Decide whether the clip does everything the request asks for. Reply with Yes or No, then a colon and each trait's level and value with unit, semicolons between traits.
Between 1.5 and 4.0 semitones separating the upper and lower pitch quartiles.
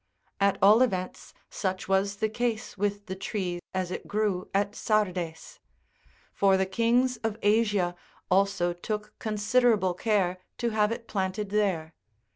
Yes: narrow, 2.5 semitones